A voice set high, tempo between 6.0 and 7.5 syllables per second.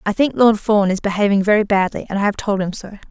Yes: high, 205 Hz; 6.3 syllables/s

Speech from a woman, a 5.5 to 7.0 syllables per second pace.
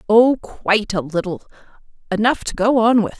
No: female; 5.1 syllables/s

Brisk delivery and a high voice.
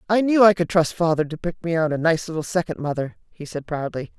No: fast, 260 wpm; medium, 165 Hz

